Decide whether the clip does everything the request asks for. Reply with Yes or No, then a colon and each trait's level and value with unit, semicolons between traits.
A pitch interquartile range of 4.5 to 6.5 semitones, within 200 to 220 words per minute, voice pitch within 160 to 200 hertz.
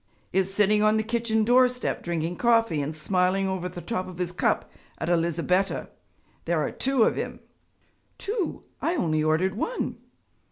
No: average, 4.8 semitones; average, 160 wpm; high, 190 Hz